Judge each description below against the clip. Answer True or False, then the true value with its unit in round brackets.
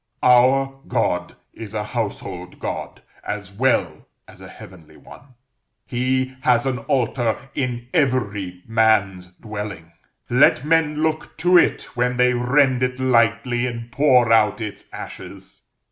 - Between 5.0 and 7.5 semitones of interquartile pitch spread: False (3.4 semitones)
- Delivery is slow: True (130 wpm)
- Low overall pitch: True (120 Hz)